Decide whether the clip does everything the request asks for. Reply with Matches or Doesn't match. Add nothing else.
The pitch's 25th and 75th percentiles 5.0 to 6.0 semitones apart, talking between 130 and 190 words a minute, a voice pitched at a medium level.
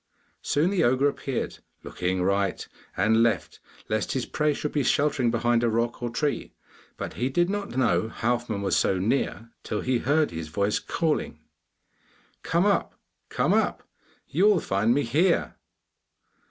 Doesn't match